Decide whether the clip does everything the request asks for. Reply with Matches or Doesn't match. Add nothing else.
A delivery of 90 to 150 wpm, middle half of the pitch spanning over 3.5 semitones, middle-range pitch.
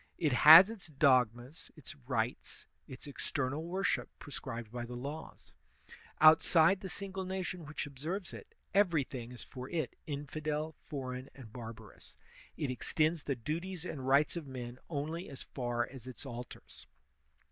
Matches